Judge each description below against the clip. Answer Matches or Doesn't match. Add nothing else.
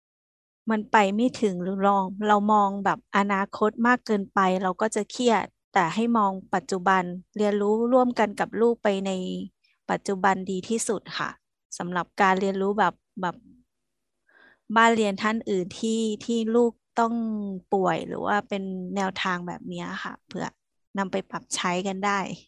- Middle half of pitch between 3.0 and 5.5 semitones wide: Doesn't match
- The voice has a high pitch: Matches